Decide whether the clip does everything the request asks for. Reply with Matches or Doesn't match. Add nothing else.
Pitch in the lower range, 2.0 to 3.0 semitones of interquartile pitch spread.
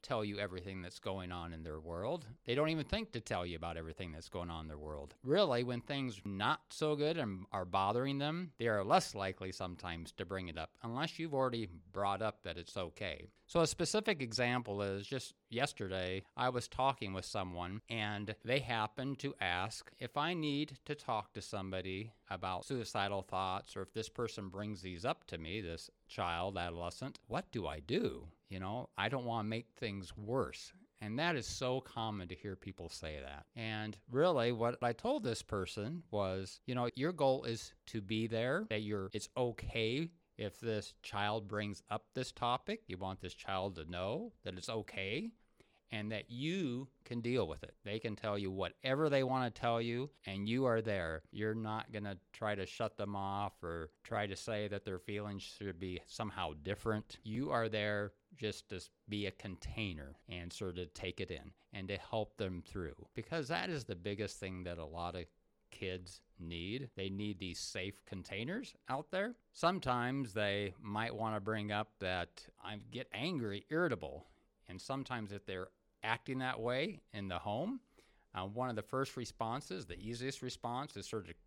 Doesn't match